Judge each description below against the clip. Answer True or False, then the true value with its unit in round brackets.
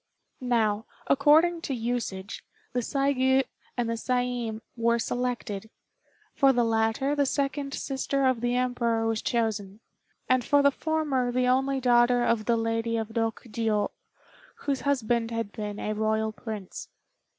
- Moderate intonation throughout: True (3.0 semitones)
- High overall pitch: True (240 Hz)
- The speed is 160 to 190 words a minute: False (140 wpm)